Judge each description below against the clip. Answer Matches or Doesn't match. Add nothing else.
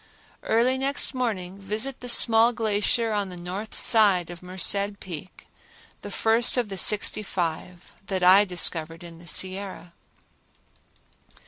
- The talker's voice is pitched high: Matches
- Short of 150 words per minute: Matches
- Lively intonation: Doesn't match